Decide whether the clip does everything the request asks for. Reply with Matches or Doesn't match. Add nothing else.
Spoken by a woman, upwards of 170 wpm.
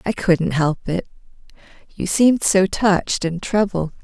Doesn't match